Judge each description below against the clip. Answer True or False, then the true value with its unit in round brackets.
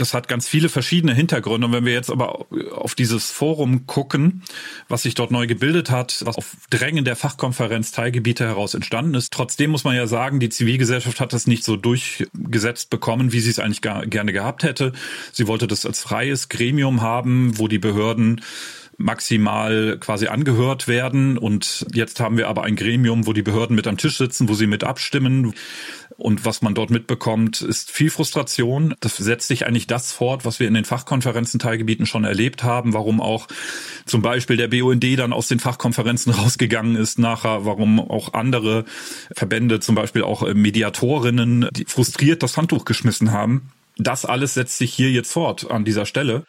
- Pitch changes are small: True (2.3 semitones)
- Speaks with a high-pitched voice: False (120 Hz)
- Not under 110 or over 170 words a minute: False (185 wpm)